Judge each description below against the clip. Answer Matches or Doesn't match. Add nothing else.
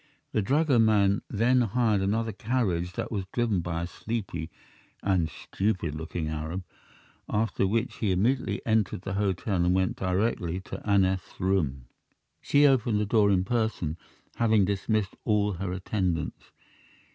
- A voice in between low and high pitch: Doesn't match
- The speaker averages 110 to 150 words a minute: Matches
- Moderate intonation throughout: Matches